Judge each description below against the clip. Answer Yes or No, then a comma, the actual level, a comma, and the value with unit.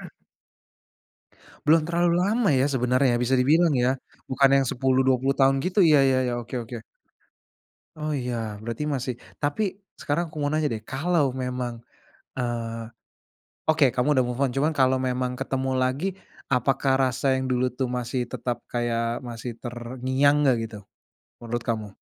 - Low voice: Yes, low, 130 Hz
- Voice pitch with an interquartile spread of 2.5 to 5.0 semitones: Yes, average, 2.9 semitones